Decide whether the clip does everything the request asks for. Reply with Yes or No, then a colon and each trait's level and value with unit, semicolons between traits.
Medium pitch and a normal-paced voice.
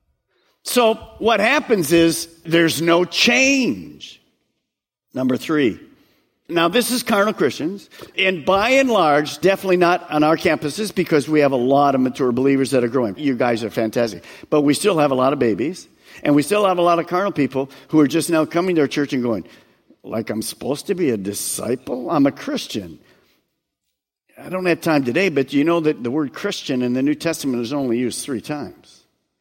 Yes: medium, 150 Hz; average, 195 wpm